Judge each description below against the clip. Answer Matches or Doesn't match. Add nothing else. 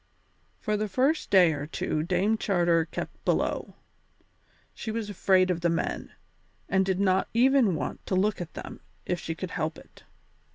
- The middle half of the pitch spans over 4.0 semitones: Doesn't match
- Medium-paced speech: Matches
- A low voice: Doesn't match